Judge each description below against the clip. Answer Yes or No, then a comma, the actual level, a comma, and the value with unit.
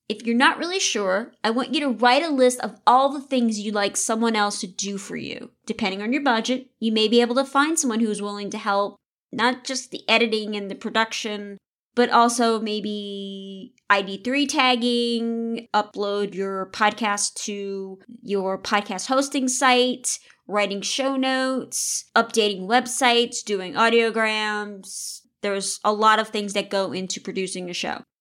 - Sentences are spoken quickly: No, average, 165 wpm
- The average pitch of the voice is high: Yes, high, 220 Hz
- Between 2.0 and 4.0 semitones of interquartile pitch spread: Yes, average, 3.5 semitones